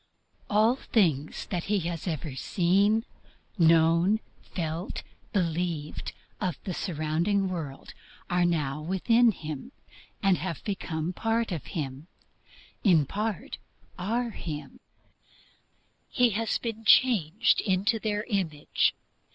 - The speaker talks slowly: Yes, slow, 105 wpm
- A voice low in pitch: No, medium, 180 Hz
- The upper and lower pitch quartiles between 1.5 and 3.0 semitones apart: No, average, 4.8 semitones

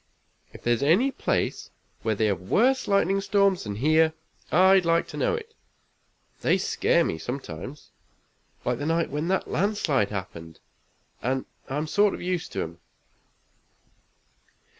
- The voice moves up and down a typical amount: No, wide, 8.9 semitones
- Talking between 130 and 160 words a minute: Yes, average, 140 wpm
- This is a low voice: No, medium, 160 Hz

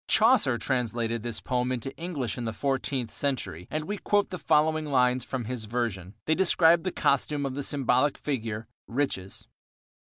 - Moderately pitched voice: No, low, 130 Hz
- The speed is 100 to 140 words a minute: No, average, 165 wpm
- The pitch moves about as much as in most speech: Yes, average, 4.4 semitones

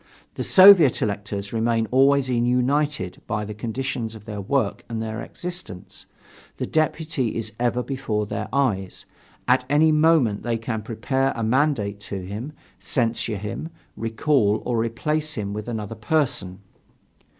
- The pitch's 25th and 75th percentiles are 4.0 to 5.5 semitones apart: Yes, average, 4.6 semitones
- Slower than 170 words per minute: Yes, average, 140 wpm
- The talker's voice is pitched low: Yes, low, 115 Hz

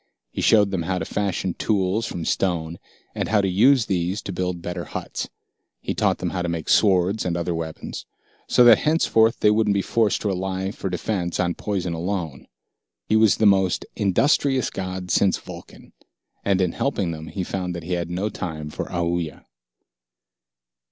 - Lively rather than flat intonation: No, average, 3.0 semitones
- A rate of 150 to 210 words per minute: Yes, average, 180 wpm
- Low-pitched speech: Yes, very low, 95 Hz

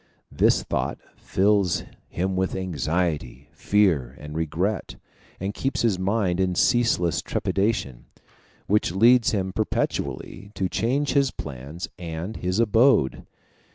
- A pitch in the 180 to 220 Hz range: No, very low, 95 Hz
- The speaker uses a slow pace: Yes, slow, 120 wpm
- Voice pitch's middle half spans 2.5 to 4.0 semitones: No, average, 4.5 semitones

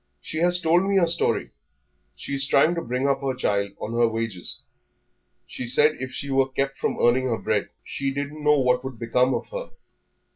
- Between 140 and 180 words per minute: No, fast, 205 wpm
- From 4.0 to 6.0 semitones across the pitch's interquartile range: No, average, 3.3 semitones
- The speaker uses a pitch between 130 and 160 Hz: Yes, low, 135 Hz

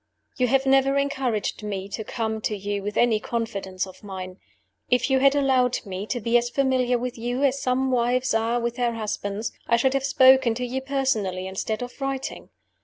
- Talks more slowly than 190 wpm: No, average, 195 wpm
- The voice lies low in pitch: No, high, 240 Hz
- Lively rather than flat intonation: No, average, 3.7 semitones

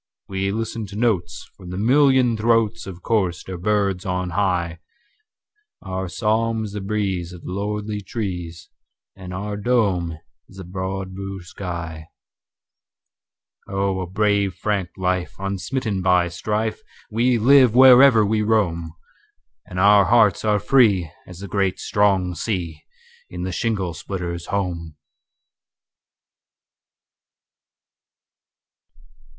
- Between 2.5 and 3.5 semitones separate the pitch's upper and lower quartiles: Yes, average, 3.1 semitones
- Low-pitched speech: Yes, low, 100 Hz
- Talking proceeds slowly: Yes, slow, 105 wpm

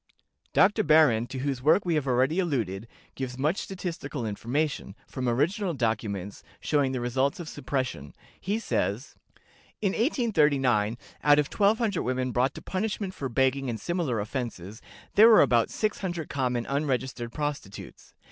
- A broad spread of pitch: Yes, wide, 5.7 semitones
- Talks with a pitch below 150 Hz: Yes, low, 135 Hz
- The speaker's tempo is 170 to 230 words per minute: No, average, 145 wpm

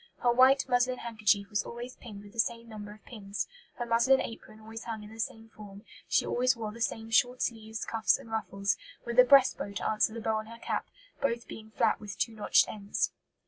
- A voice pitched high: Yes, high, 225 Hz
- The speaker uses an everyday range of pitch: No, narrow, 2.0 semitones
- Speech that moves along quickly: Yes, fast, 225 wpm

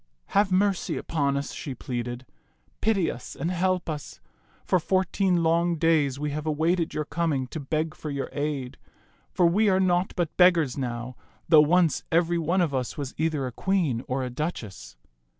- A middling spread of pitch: Yes, average, 4.4 semitones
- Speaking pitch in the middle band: Yes, medium, 155 Hz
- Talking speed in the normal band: Yes, average, 185 wpm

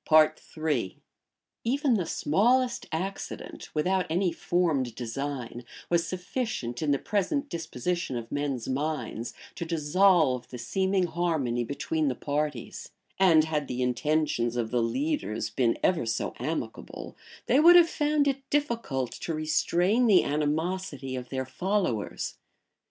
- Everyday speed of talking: No, slow, 130 wpm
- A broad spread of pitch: Yes, wide, 6.6 semitones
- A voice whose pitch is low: No, medium, 155 Hz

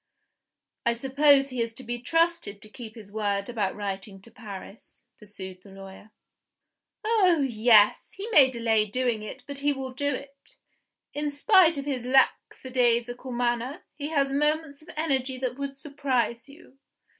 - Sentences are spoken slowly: No, average, 155 wpm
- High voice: Yes, very high, 255 Hz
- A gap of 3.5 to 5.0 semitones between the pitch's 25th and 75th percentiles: Yes, average, 4.2 semitones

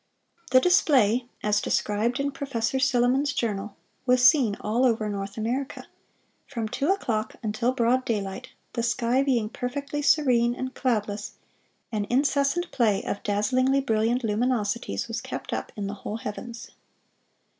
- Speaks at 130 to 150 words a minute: Yes, average, 140 wpm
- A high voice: Yes, high, 240 Hz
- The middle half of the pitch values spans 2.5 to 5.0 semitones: Yes, average, 3.6 semitones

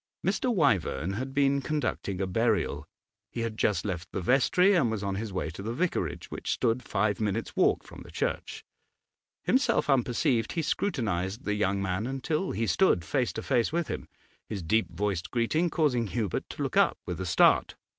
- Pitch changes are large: Yes, wide, 5.9 semitones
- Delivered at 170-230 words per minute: Yes, average, 185 wpm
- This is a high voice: No, low, 115 Hz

